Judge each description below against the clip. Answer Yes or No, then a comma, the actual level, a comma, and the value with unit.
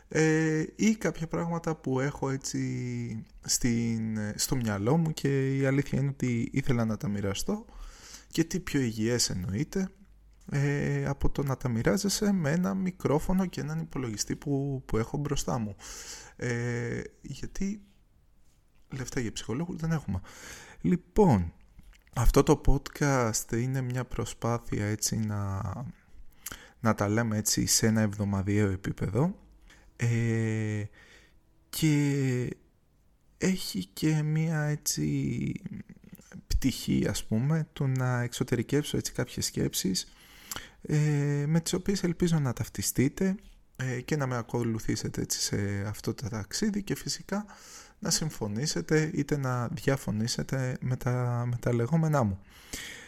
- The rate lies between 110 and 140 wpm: Yes, average, 120 wpm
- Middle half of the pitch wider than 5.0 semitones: Yes, wide, 5.6 semitones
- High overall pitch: No, low, 135 Hz